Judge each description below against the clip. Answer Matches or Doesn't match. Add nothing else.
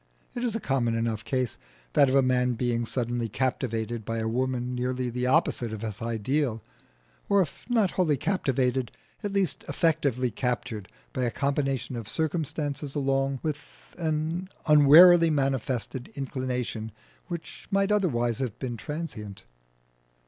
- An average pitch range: Matches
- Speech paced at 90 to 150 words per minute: Matches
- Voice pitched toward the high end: Doesn't match